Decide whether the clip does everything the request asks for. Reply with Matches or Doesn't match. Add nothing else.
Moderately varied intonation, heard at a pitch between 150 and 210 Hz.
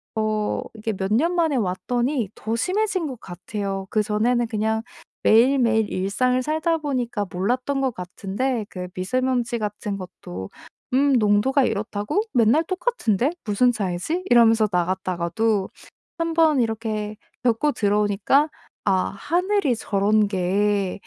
Doesn't match